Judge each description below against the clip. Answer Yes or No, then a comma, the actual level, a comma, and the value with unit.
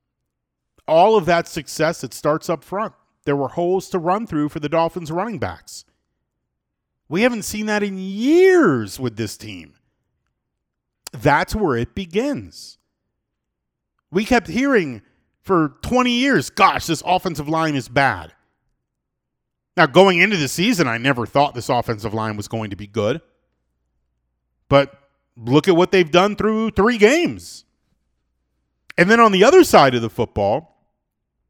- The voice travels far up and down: Yes, wide, 9.0 semitones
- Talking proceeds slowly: No, average, 150 wpm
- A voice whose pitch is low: No, medium, 150 Hz